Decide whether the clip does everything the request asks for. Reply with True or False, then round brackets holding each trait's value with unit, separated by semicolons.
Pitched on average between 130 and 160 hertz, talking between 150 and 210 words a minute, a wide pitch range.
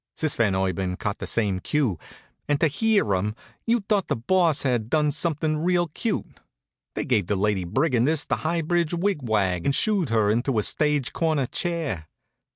True (140 Hz; 180 wpm; 7.8 semitones)